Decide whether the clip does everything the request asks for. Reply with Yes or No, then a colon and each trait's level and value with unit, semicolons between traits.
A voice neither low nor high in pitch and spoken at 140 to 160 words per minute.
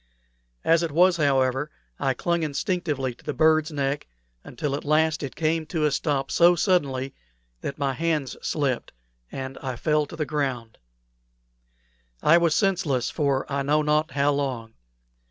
Yes: medium, 150 Hz; average, 155 wpm